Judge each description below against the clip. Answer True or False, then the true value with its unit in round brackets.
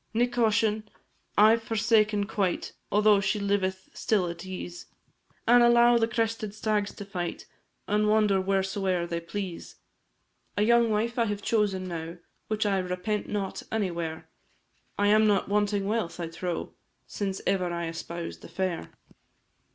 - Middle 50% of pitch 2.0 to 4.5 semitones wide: True (2.8 semitones)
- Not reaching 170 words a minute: True (150 wpm)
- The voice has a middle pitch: False (205 Hz)